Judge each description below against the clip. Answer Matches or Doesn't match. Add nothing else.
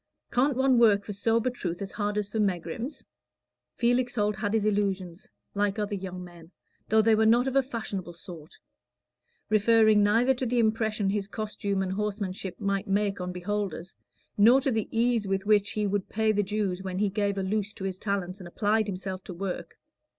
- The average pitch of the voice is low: Doesn't match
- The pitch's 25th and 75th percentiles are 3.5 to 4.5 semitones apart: Doesn't match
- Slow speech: Doesn't match